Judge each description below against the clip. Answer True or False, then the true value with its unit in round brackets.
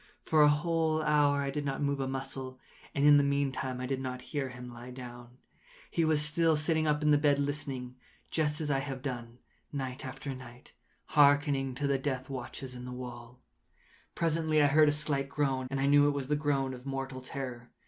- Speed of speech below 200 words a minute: False (205 wpm)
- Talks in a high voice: False (140 Hz)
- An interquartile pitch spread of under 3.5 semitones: True (2.4 semitones)